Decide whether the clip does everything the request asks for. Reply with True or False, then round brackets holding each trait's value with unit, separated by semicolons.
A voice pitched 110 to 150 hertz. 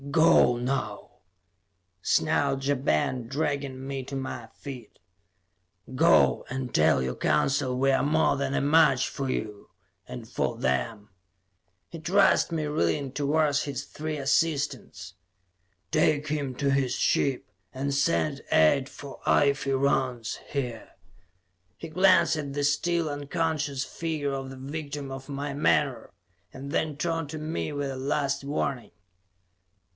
True (140 Hz)